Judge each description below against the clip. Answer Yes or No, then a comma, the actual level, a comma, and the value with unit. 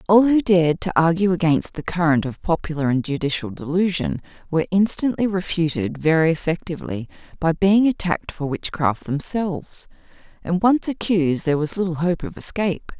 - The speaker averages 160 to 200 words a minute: No, average, 150 wpm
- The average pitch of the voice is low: No, medium, 170 Hz